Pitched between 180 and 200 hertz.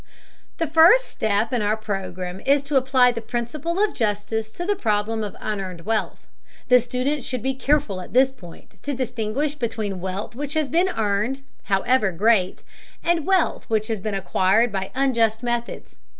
No: high, 230 Hz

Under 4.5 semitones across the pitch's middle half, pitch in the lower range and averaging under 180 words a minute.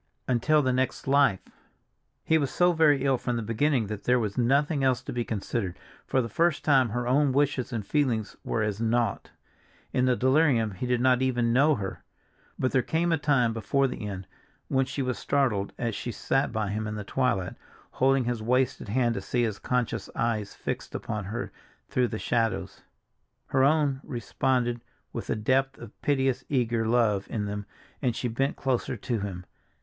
No: average, 3.3 semitones; low, 125 Hz; average, 190 wpm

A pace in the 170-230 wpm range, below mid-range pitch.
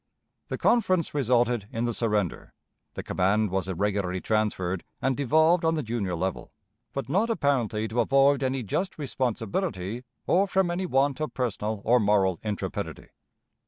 No: average, 150 wpm; low, 120 Hz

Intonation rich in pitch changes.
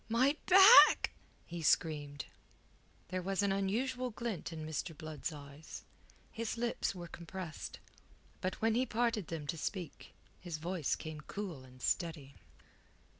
Yes: wide, 6.1 semitones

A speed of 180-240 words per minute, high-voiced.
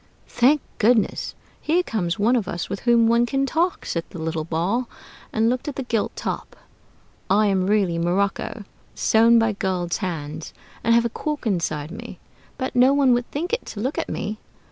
Yes: average, 190 wpm; high, 220 Hz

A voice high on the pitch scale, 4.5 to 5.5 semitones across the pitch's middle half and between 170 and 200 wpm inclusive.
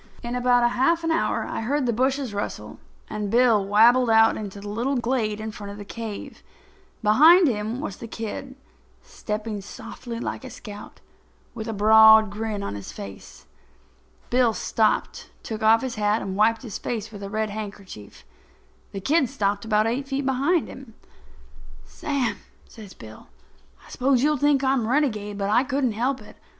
No: high, 225 Hz; average, 3.6 semitones; average, 175 wpm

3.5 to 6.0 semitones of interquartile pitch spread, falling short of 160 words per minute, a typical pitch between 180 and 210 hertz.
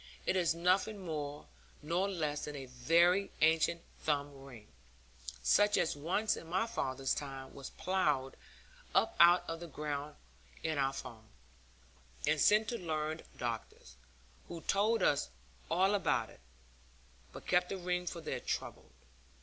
No: average, 4.2 semitones; average, 145 wpm; medium, 160 Hz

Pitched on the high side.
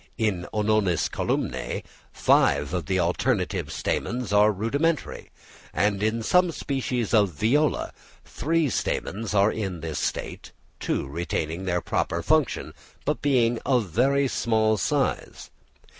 No: low, 110 Hz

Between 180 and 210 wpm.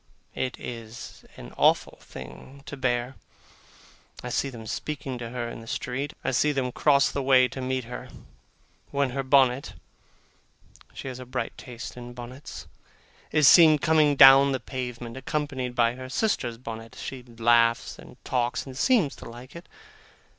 No: average, 160 wpm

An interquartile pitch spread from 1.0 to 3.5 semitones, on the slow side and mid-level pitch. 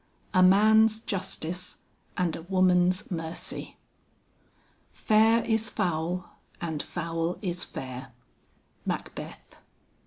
Yes: average, 3.1 semitones; slow, 90 wpm; medium, 180 Hz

